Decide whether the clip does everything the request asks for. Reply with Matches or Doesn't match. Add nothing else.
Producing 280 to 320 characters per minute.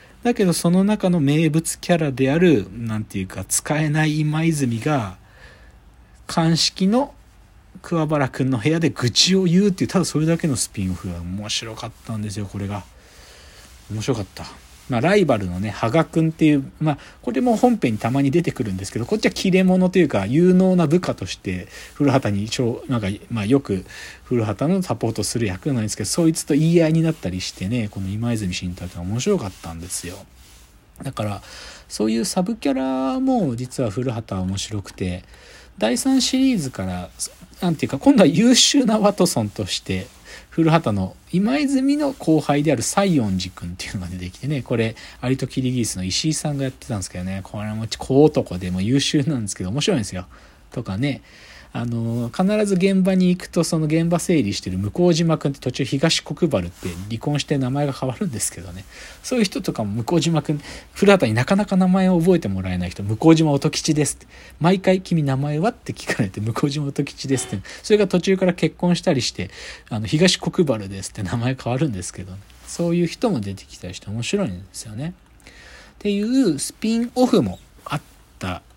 Doesn't match